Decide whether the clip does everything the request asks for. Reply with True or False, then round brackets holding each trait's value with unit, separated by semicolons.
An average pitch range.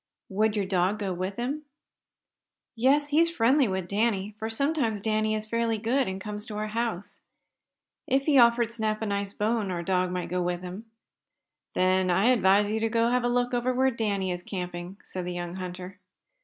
True (3.9 semitones)